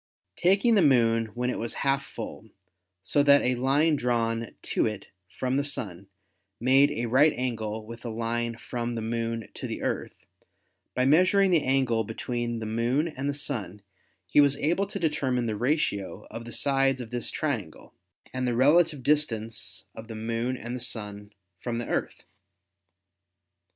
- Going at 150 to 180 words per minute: Yes, average, 170 wpm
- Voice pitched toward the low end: Yes, low, 120 Hz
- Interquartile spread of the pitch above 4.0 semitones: No, average, 3.7 semitones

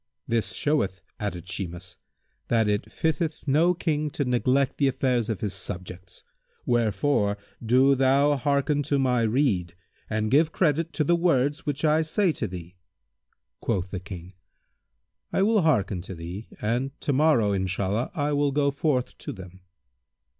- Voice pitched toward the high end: No, low, 125 Hz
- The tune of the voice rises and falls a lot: Yes, wide, 6.7 semitones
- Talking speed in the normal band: Yes, average, 155 wpm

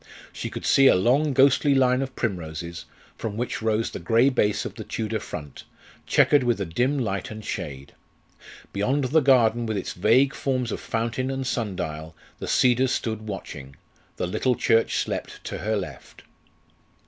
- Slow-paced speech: No, average, 170 wpm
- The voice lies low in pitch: Yes, low, 115 Hz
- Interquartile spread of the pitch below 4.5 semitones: No, average, 4.9 semitones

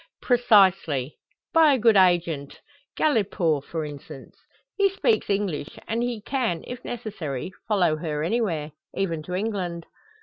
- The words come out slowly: Yes, slow, 130 wpm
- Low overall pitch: No, high, 190 Hz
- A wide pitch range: Yes, wide, 6.5 semitones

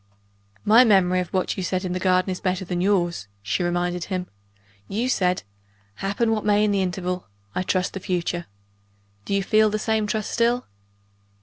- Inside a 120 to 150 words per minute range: No, average, 185 wpm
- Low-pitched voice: No, medium, 185 Hz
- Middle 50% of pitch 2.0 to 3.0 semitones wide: Yes, narrow, 2.6 semitones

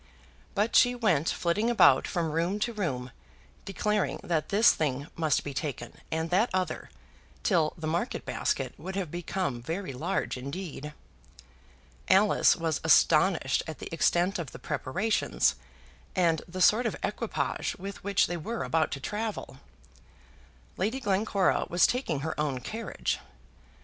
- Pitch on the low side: No, medium, 175 Hz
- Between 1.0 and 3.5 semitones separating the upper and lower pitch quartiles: No, average, 4.6 semitones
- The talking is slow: No, average, 145 wpm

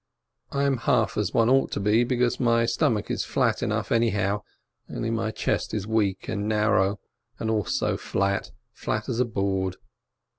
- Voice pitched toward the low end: Yes, low, 110 Hz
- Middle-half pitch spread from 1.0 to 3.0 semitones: Yes, narrow, 2.5 semitones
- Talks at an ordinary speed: Yes, average, 175 wpm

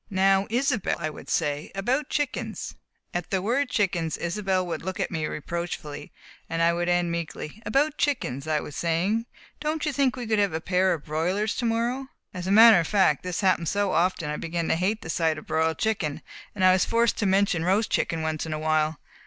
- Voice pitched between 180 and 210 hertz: Yes, medium, 185 Hz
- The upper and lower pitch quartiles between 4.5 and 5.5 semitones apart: Yes, average, 5.1 semitones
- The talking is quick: Yes, fast, 225 wpm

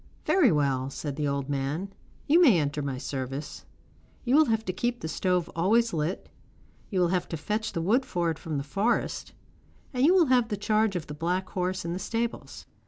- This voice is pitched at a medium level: Yes, medium, 180 Hz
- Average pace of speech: No, fast, 210 wpm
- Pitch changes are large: Yes, wide, 7.1 semitones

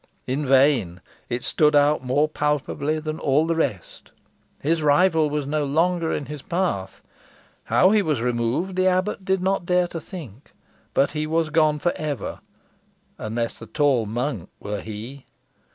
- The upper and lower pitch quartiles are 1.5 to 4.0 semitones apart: No, average, 4.4 semitones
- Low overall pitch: No, medium, 150 Hz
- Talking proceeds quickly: No, average, 160 wpm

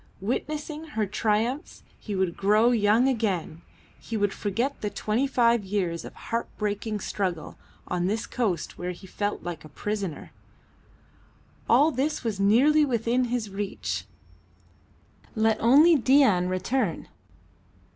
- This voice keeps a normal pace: No, slow, 130 wpm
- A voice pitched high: Yes, high, 215 Hz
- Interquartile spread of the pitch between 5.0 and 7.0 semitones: No, average, 4.2 semitones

